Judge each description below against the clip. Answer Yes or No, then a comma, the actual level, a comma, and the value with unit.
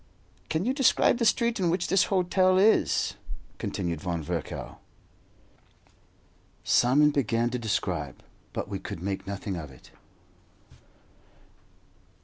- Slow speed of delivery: Yes, slow, 120 wpm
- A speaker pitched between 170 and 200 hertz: No, low, 120 Hz